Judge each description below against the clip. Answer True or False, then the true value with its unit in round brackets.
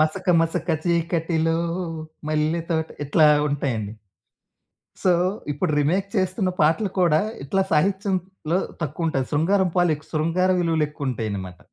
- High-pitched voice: False (160 Hz)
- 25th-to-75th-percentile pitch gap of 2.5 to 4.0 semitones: True (3.3 semitones)